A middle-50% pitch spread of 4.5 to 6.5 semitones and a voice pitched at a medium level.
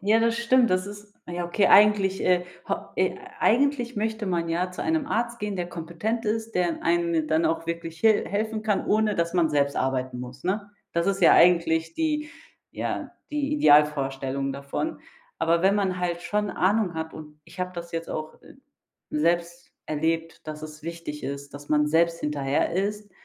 Yes: average, 4.8 semitones; medium, 175 Hz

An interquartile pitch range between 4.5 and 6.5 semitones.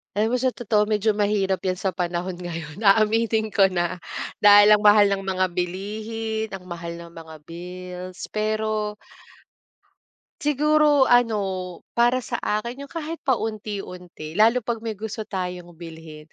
No: average, 3.6 semitones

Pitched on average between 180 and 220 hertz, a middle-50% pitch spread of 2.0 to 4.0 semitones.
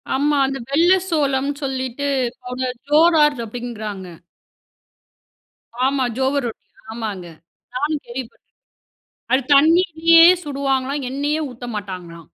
No: very high, 270 Hz; average, 3.5 semitones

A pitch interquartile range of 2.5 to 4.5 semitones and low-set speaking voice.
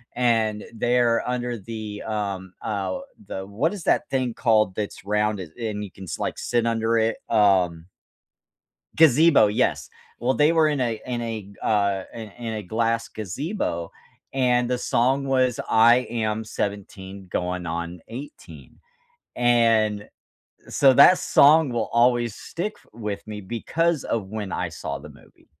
Yes: average, 3.2 semitones; low, 115 Hz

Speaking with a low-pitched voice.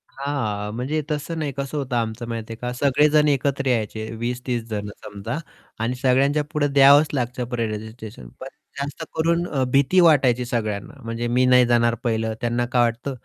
Yes: low, 125 Hz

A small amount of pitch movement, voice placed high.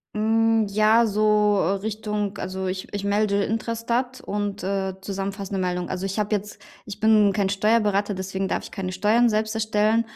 Yes: narrow, 1.9 semitones; high, 210 Hz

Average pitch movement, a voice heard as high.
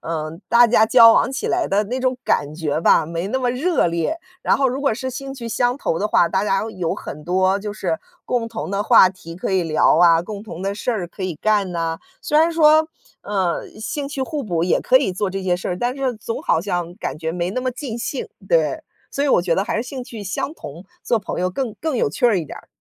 No: wide, 6.4 semitones; high, 205 Hz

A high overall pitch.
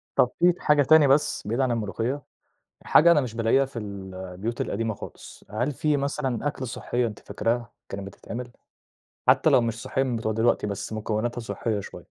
No: low, 120 Hz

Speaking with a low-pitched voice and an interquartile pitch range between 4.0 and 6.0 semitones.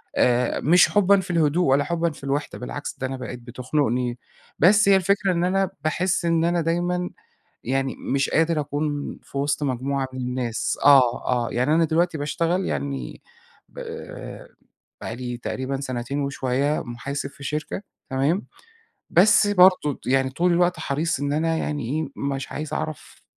No: medium, 145 Hz; average, 4.5 semitones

